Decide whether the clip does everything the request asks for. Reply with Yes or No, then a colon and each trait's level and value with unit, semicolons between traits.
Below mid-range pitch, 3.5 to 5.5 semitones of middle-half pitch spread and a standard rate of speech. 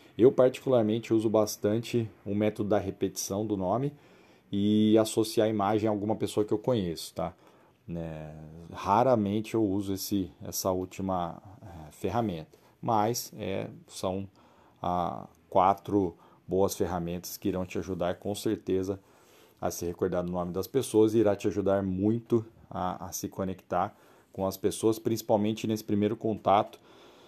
No: low, 100 Hz; average, 2.9 semitones; average, 145 wpm